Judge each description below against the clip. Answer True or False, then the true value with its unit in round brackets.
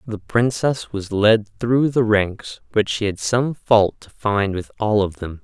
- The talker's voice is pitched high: False (110 Hz)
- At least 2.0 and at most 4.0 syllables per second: True (3.8 syllables/s)